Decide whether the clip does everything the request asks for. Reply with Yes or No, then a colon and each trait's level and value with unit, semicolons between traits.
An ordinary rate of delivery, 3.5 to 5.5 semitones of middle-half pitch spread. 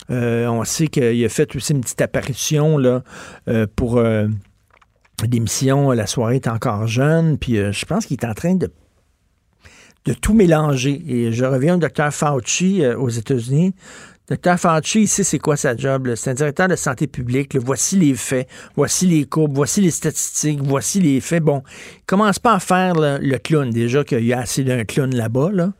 Yes: average, 200 wpm; average, 4.7 semitones